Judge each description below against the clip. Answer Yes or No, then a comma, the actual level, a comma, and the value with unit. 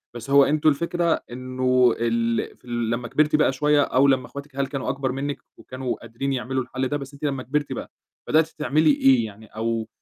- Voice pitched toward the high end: No, low, 135 Hz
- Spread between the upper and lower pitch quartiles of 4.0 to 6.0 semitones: No, average, 2.8 semitones